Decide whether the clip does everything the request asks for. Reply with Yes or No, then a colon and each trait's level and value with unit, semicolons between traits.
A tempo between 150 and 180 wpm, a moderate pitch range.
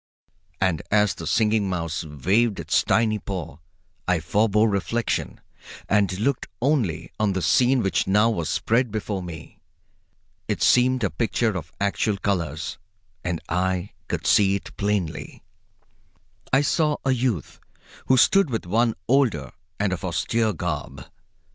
No: average, 140 wpm; average, 4.6 semitones